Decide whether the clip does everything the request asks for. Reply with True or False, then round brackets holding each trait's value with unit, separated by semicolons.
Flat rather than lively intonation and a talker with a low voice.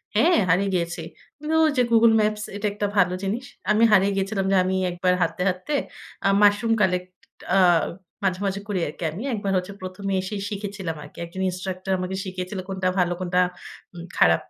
False (2.2 semitones; 190 Hz)